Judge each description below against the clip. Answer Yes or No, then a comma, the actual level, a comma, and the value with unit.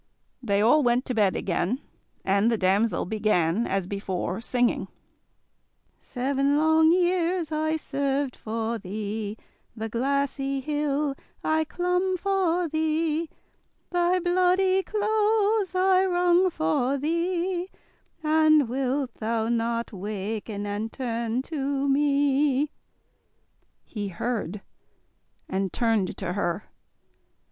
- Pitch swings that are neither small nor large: No, wide, 7.0 semitones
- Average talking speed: No, slow, 105 wpm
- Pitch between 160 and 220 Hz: No, very high, 275 Hz